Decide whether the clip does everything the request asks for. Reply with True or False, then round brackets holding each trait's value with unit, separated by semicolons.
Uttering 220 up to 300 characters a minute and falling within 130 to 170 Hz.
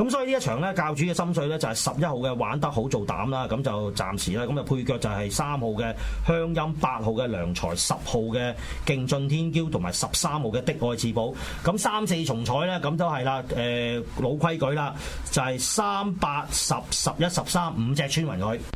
True (295 characters per minute; 140 Hz)